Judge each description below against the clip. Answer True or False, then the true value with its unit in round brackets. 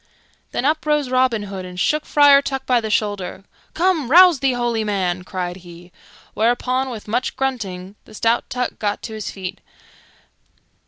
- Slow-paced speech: False (165 wpm)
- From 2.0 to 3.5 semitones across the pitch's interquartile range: False (5.4 semitones)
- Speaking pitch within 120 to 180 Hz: False (230 Hz)